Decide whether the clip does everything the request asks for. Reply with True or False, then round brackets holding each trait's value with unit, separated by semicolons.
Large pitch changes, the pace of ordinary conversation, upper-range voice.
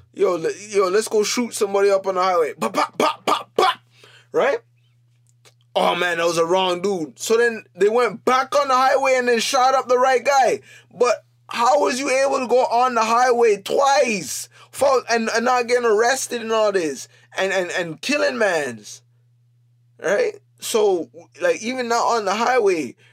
True (6.9 semitones; 180 wpm; 225 Hz)